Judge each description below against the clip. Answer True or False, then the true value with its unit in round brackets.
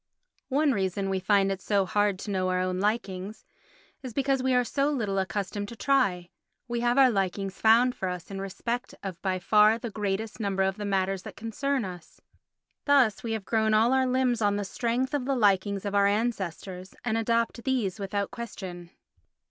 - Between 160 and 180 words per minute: False (195 wpm)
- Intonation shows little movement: False (3.7 semitones)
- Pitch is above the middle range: True (205 Hz)